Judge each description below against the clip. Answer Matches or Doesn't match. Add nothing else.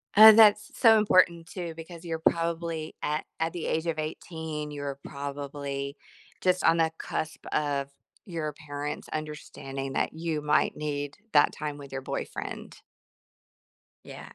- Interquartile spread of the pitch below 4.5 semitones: Matches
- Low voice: Doesn't match